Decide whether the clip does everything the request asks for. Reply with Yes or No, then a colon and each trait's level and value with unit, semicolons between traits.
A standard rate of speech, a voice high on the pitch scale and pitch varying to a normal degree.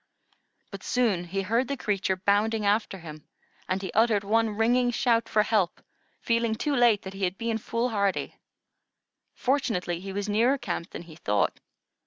Yes: average, 165 wpm; high, 210 Hz; average, 3.4 semitones